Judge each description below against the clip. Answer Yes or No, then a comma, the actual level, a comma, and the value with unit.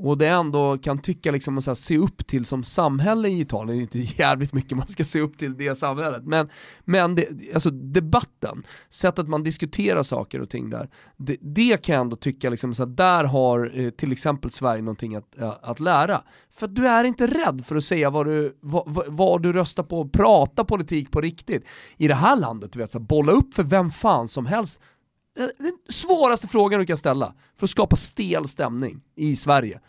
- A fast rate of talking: Yes, fast, 205 wpm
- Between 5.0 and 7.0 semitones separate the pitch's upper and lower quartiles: Yes, wide, 5.5 semitones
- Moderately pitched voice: Yes, medium, 150 Hz